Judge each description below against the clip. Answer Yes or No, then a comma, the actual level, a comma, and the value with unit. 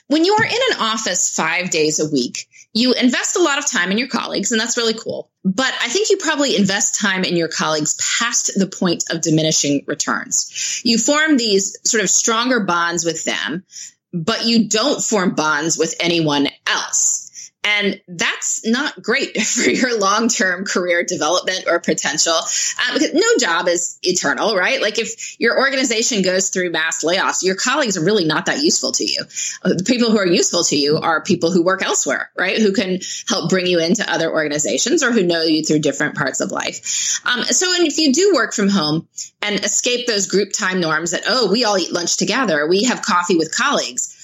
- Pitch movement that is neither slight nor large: No, wide, 5.7 semitones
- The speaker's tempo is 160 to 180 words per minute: No, average, 200 wpm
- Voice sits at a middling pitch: No, high, 200 Hz